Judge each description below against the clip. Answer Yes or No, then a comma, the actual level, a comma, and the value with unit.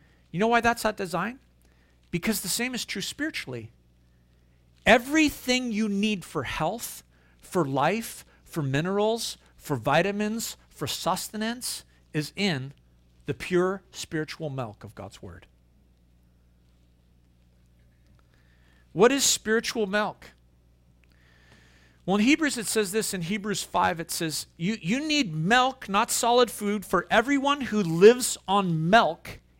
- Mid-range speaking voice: Yes, medium, 170 Hz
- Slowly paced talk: Yes, slow, 125 wpm